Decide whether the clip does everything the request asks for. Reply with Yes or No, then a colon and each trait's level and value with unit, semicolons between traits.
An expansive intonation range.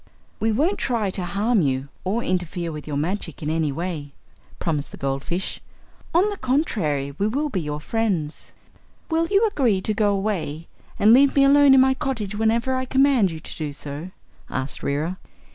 Yes: wide, 8.9 semitones